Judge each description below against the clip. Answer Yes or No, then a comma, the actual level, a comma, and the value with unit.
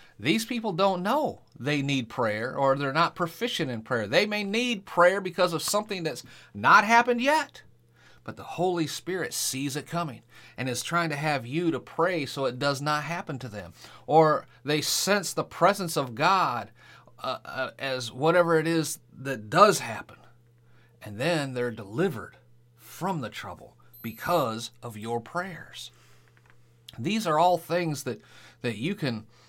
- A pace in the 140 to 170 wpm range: Yes, average, 165 wpm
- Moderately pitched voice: Yes, medium, 150 Hz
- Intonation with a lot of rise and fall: Yes, wide, 6.2 semitones